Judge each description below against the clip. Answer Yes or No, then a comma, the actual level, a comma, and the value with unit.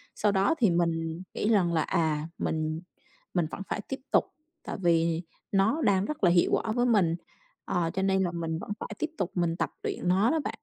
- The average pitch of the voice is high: No, medium, 180 Hz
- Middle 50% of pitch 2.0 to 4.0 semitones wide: Yes, average, 3.5 semitones